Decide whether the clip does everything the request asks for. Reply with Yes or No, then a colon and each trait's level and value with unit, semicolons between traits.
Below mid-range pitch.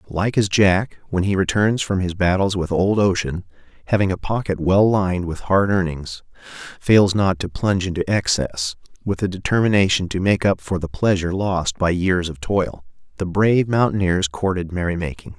Yes: very low, 95 Hz